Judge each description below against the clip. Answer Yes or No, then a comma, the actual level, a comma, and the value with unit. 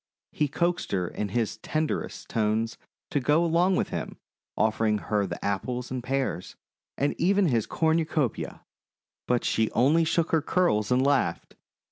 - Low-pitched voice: Yes, low, 130 Hz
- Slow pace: No, average, 150 wpm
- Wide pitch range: Yes, wide, 6.6 semitones